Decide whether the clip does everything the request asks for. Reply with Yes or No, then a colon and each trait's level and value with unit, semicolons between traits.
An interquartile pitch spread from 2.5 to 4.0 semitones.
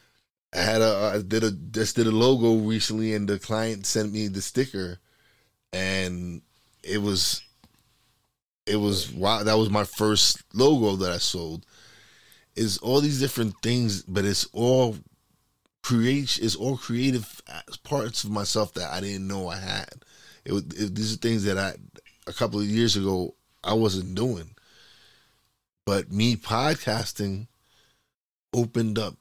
Yes: average, 2.9 semitones